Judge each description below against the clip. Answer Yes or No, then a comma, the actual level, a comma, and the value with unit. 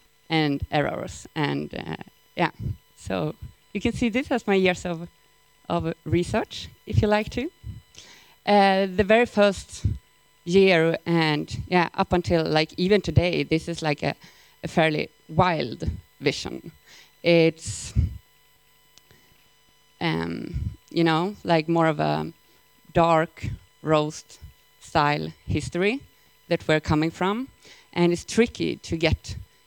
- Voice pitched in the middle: Yes, medium, 165 Hz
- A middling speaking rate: No, slow, 125 wpm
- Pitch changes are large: No, average, 5.0 semitones